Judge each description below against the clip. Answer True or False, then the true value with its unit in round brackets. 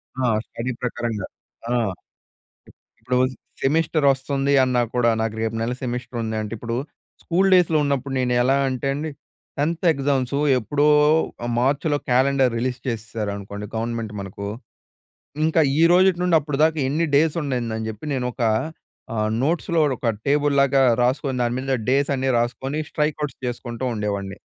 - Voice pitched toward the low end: True (130 Hz)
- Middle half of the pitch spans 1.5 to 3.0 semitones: False (3.7 semitones)